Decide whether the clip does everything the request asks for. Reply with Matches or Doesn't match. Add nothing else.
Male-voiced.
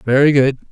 Matches